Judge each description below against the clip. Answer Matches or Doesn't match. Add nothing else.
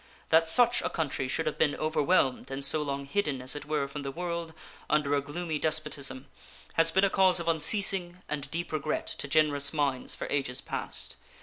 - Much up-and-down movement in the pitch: Doesn't match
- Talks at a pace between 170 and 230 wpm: Matches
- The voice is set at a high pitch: Doesn't match